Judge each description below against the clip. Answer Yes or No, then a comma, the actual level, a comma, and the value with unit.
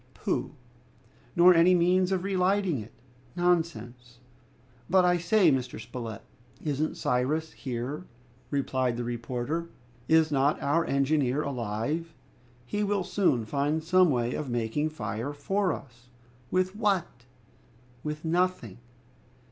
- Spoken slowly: Yes, slow, 125 wpm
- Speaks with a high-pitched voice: No, medium, 150 Hz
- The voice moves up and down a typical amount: No, wide, 6.2 semitones